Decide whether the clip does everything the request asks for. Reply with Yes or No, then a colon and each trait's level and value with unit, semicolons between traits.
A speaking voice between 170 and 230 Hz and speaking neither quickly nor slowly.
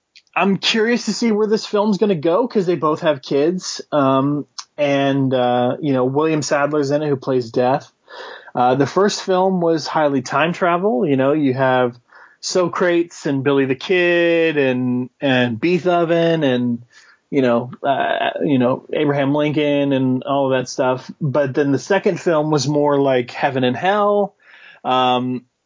No: medium, 145 Hz; average, 170 wpm